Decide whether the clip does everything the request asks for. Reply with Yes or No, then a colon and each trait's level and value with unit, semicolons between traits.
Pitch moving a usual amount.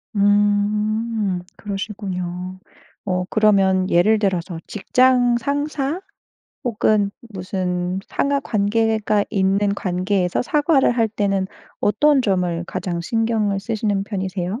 Yes: average, 3.1 semitones